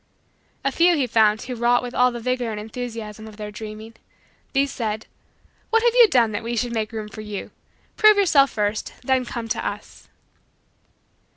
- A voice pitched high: Yes, high, 235 Hz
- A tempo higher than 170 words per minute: Yes, average, 185 wpm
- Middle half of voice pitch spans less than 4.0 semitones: Yes, average, 3.2 semitones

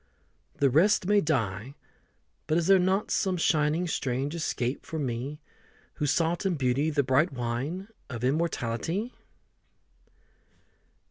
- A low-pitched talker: No, medium, 150 Hz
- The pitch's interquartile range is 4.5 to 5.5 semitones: Yes, average, 5.0 semitones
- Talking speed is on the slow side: Yes, slow, 125 wpm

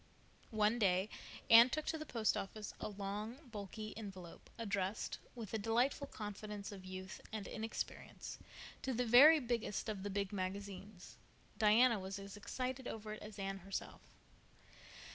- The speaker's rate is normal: Yes, average, 150 wpm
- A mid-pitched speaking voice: No, high, 210 Hz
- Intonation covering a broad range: No, average, 2.7 semitones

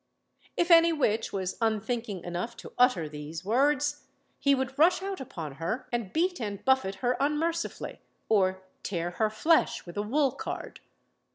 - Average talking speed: Yes, average, 160 wpm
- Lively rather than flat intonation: Yes, wide, 7.5 semitones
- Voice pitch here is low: No, high, 235 Hz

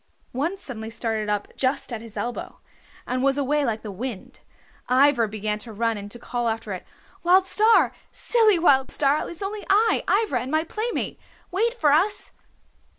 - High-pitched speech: Yes, very high, 265 Hz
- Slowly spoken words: No, average, 175 wpm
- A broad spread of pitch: Yes, wide, 8.1 semitones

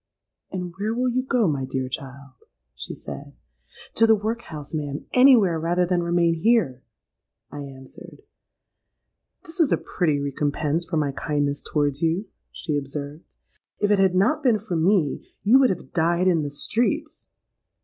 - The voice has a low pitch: No, medium, 170 Hz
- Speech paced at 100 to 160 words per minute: Yes, average, 150 wpm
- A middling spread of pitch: No, wide, 6.8 semitones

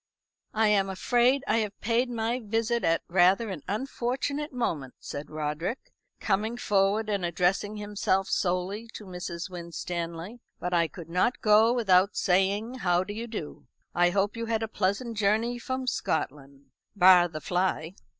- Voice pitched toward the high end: Yes, high, 200 Hz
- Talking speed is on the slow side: No, average, 155 wpm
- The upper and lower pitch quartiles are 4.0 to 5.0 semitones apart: Yes, average, 4.4 semitones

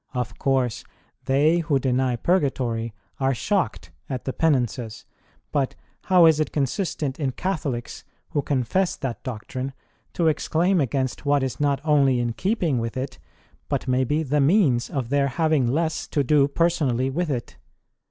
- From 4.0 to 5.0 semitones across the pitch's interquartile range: No, average, 3.6 semitones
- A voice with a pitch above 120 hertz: Yes, medium, 140 Hz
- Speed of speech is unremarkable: Yes, average, 155 wpm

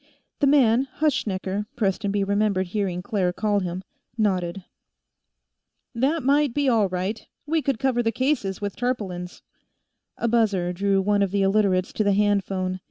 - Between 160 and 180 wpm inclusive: No, average, 150 wpm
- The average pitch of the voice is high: Yes, high, 205 Hz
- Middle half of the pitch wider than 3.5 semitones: Yes, average, 4.0 semitones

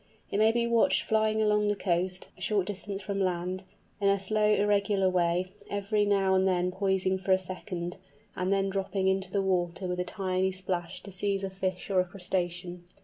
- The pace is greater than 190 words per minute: Yes, average, 200 wpm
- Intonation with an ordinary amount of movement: No, narrow, 1.6 semitones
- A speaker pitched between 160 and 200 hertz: Yes, high, 190 Hz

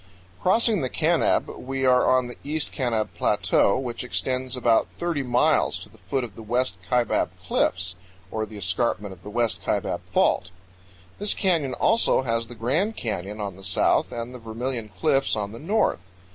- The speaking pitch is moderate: No, low, 125 Hz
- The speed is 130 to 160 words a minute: No, average, 175 wpm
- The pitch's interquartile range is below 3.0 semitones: No, average, 3.7 semitones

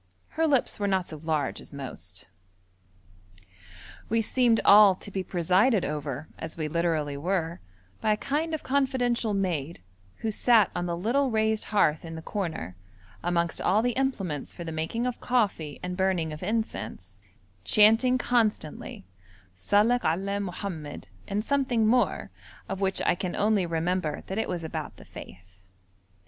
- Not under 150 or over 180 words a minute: Yes, average, 155 wpm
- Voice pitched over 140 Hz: Yes, high, 190 Hz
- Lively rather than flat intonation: Yes, wide, 5.7 semitones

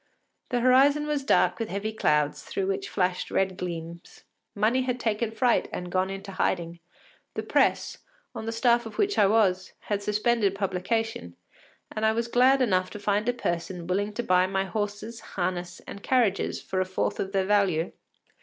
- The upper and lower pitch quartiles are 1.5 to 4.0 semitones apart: Yes, average, 3.7 semitones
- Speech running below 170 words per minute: No, average, 180 wpm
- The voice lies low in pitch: No, high, 205 Hz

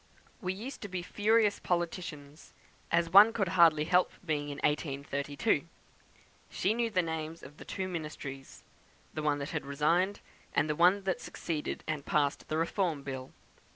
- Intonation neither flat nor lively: Yes, average, 4.2 semitones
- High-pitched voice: No, medium, 165 Hz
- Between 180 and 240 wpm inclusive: No, average, 155 wpm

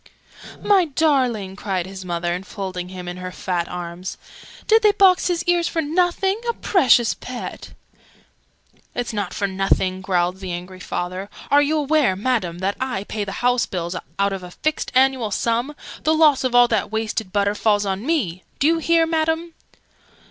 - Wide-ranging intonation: Yes, wide, 8.6 semitones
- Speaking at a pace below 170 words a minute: No, average, 175 wpm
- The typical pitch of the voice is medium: No, high, 220 Hz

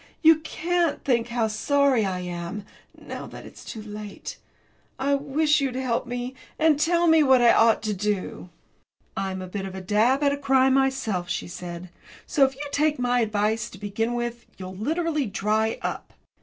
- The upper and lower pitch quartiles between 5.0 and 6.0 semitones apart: Yes, average, 5.3 semitones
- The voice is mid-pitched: No, high, 240 Hz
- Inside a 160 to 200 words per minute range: Yes, average, 185 wpm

